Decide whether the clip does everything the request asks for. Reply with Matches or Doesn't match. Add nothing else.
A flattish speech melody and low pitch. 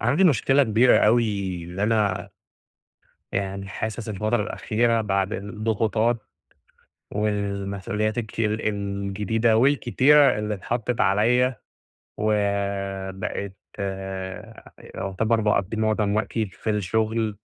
Matches